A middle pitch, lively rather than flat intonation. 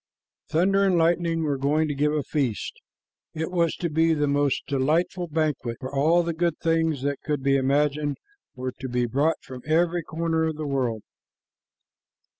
No: medium, 150 Hz; average, 3.0 semitones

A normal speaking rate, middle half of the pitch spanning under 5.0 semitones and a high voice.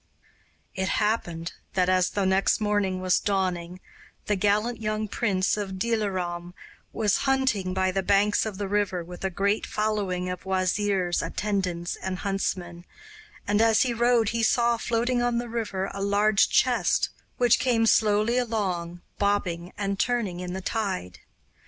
Yes: average, 150 wpm; average, 2.9 semitones; high, 200 Hz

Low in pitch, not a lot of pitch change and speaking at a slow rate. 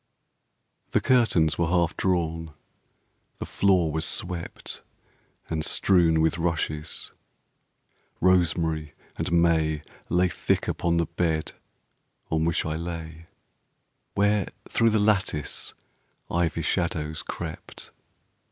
Yes: very low, 85 Hz; narrow, 2.0 semitones; slow, 105 wpm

